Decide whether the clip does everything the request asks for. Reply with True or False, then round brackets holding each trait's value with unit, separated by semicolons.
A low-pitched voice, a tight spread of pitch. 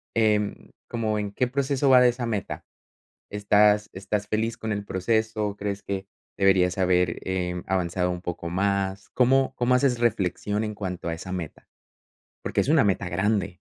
False (105 Hz; 3.1 semitones)